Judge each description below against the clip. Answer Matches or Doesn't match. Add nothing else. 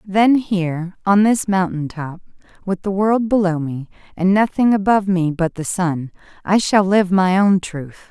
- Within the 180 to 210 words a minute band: Doesn't match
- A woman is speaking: Matches